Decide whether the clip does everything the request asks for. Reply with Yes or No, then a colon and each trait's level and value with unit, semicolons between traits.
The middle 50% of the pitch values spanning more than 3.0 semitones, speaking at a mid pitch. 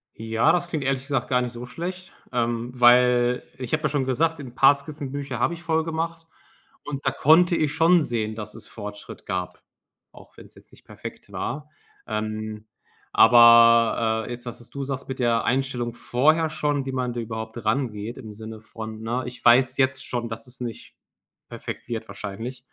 No: average, 3.6 semitones; low, 125 Hz